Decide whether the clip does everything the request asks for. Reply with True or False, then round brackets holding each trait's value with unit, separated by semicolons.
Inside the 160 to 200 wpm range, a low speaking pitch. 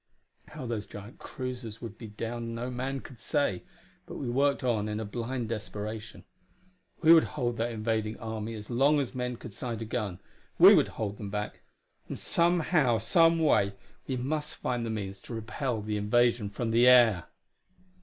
True (175 wpm; 115 Hz)